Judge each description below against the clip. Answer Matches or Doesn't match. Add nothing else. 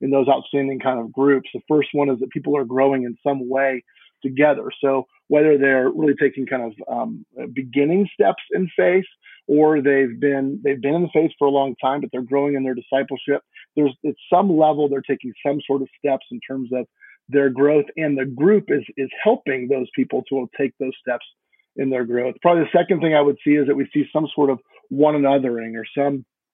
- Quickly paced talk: Matches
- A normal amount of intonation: Doesn't match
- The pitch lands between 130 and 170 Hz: Matches